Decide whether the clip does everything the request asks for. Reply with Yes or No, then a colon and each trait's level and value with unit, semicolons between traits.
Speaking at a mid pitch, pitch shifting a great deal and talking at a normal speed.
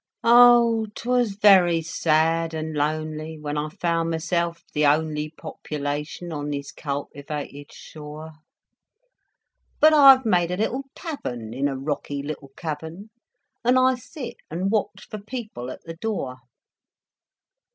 No: medium, 165 Hz; wide, 6.3 semitones; slow, 130 wpm